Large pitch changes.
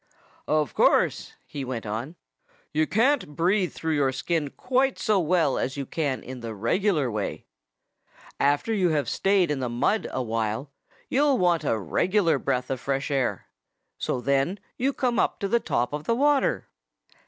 Yes: wide, 7.1 semitones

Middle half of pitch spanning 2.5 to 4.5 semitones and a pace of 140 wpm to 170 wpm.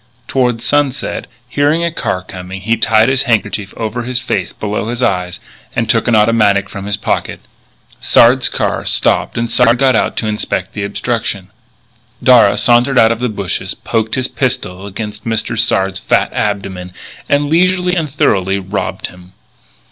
Yes: average, 4.1 semitones; average, 165 wpm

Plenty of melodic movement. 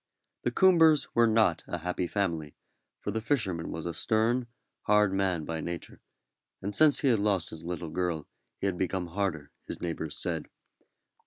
No: average, 4.7 semitones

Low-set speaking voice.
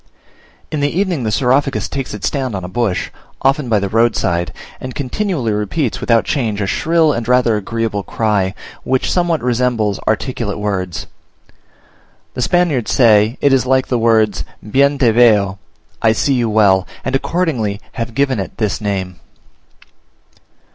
Yes: low, 115 Hz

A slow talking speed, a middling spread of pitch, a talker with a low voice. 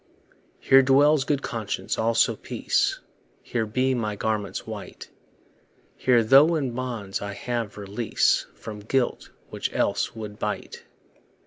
Yes: slow, 125 wpm; average, 3.9 semitones; low, 115 Hz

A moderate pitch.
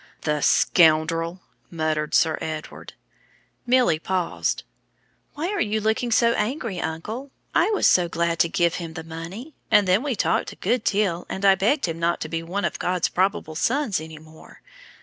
Yes: medium, 180 Hz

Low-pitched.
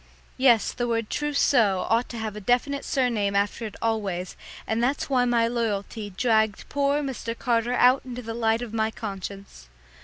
No: high, 230 Hz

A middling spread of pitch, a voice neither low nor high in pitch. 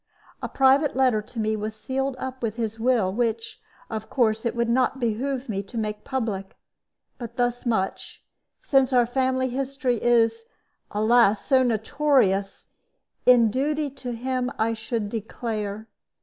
No: average, 3.0 semitones; high, 235 Hz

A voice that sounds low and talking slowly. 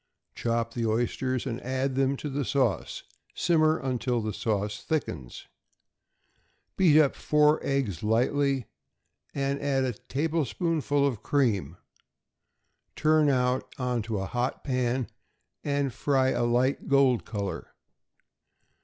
Yes: low, 130 Hz; slow, 120 wpm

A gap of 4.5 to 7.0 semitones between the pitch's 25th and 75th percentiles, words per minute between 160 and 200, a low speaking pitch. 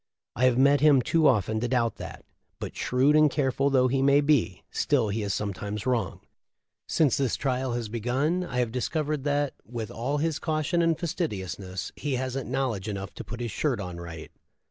Yes: average, 4.9 semitones; average, 190 wpm; low, 130 Hz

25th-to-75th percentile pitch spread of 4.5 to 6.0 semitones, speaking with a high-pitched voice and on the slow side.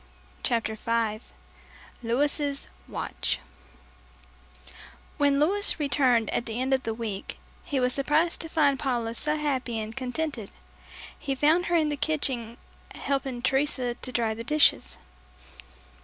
No: average, 4.1 semitones; very high, 265 Hz; slow, 130 wpm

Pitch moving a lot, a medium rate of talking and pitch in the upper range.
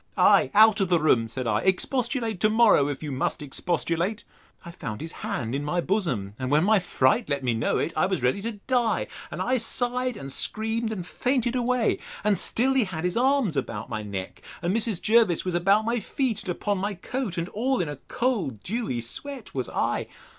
No: wide, 7.8 semitones; fast, 210 wpm; high, 195 Hz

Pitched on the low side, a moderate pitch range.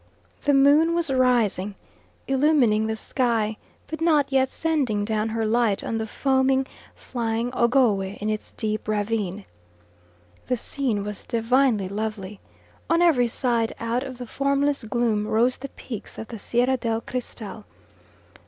No: high, 235 Hz; average, 3.7 semitones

